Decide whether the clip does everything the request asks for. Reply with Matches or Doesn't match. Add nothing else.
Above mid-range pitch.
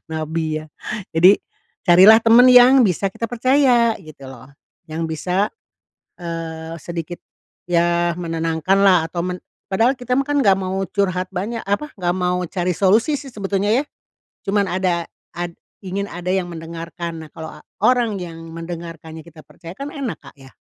Doesn't match